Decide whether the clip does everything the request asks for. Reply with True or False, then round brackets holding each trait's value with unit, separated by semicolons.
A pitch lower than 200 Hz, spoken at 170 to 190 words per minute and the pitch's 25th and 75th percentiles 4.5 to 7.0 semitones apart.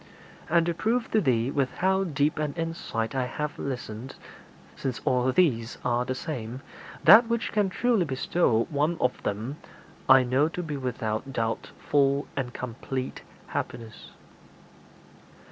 False (135 Hz; 145 wpm; 5.0 semitones)